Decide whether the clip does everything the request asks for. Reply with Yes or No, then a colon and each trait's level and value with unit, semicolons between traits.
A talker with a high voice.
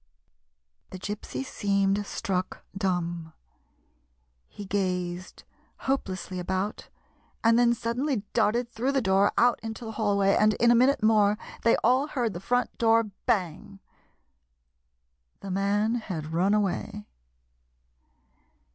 Yes: high, 205 Hz